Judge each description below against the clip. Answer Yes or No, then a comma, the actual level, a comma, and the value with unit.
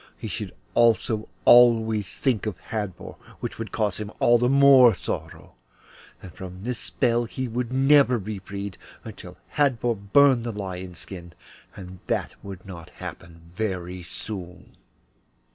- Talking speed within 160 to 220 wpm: No, average, 145 wpm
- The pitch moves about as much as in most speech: Yes, average, 4.5 semitones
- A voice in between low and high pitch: No, low, 110 Hz